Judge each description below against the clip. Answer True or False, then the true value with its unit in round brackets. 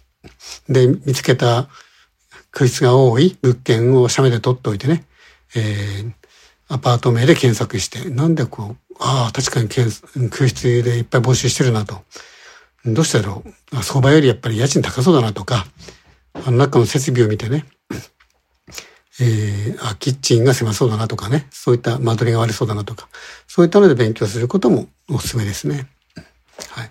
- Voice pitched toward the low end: True (125 Hz)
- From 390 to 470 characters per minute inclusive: False (325 characters per minute)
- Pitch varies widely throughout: False (2.9 semitones)